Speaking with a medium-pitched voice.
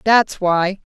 No: high, 195 Hz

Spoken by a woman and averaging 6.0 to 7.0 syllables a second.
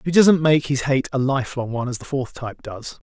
No: male; 6.4 syllables/s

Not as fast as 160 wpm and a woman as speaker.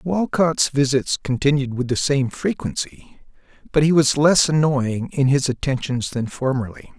No: average, 145 wpm; male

